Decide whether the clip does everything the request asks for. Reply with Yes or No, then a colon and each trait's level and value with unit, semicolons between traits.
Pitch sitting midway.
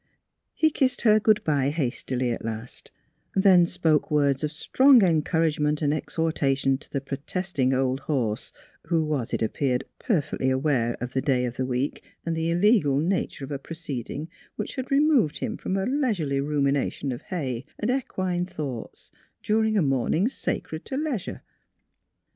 Yes: medium, 150 Hz